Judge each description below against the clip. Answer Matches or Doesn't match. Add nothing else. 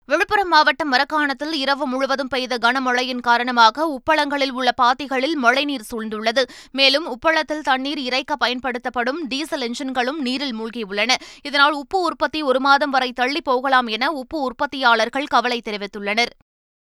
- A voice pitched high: Matches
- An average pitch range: Matches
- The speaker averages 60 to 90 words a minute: Doesn't match